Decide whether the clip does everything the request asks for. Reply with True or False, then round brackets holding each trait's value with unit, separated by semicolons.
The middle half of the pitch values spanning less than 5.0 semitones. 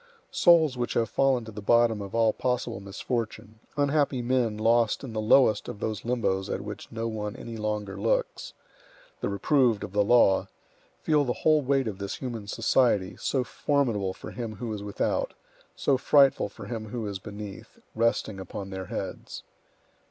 True (3.4 semitones)